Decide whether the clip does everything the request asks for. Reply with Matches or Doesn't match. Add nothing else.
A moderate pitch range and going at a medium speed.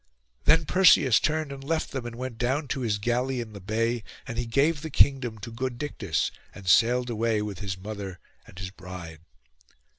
Matches